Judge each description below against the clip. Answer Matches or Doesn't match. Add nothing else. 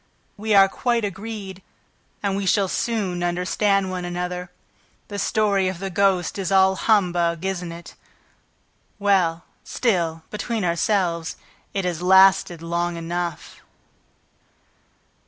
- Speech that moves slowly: Matches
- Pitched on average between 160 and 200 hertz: Matches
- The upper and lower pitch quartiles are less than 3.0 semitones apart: Matches